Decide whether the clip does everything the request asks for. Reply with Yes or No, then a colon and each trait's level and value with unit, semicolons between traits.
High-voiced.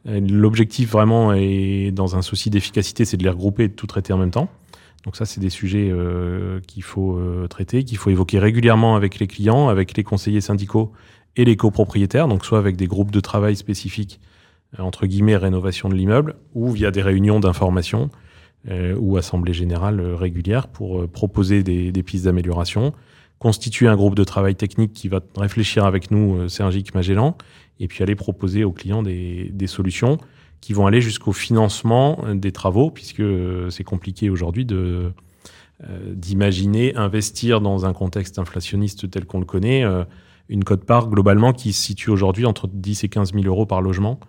No: low, 100 Hz